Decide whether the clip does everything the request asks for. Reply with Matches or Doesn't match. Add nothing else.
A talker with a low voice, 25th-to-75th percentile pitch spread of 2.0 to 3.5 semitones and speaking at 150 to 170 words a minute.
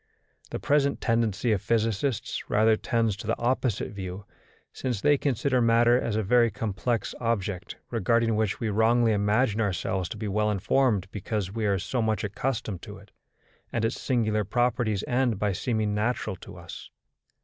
Matches